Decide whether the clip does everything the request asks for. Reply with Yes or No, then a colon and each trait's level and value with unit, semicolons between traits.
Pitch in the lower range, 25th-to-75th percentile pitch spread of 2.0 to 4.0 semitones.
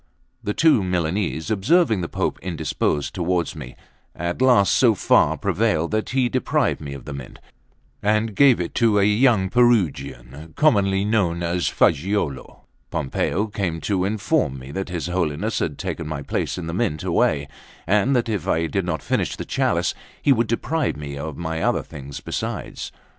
No: very low, 90 Hz; wide, 5.5 semitones